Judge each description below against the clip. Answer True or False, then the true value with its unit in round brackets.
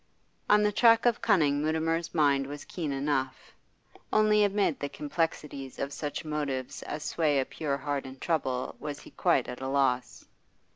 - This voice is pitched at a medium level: True (145 Hz)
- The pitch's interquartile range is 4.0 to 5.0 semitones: False (3.0 semitones)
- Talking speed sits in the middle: True (165 wpm)